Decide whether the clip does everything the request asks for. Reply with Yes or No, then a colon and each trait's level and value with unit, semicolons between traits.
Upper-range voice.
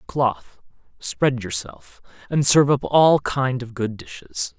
No: low, 115 Hz